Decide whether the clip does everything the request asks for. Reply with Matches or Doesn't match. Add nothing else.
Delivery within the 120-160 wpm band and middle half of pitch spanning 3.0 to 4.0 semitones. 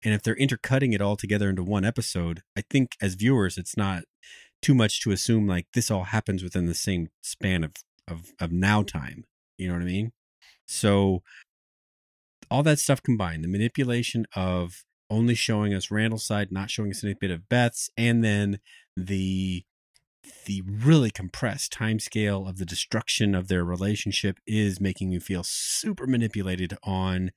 Doesn't match